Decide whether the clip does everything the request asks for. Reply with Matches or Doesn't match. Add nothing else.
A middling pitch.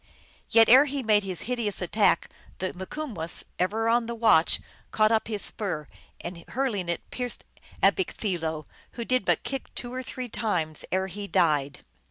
Doesn't match